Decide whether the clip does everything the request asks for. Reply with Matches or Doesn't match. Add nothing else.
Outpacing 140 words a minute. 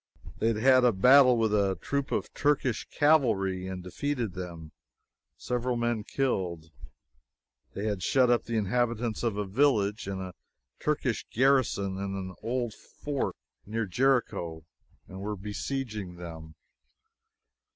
Doesn't match